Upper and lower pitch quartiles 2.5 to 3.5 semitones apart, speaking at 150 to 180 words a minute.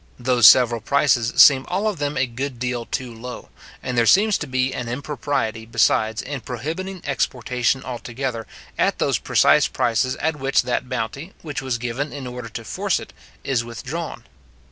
Yes: average, 3.2 semitones; average, 170 wpm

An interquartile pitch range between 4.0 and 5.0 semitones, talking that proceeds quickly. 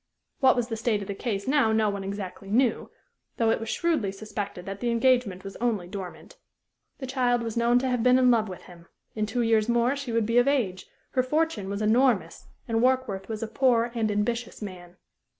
No: average, 3.6 semitones; fast, 215 wpm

